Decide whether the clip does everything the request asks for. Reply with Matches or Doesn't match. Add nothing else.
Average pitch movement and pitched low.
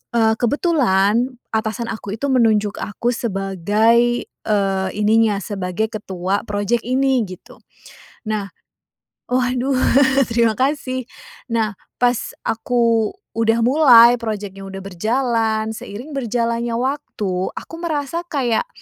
Doesn't match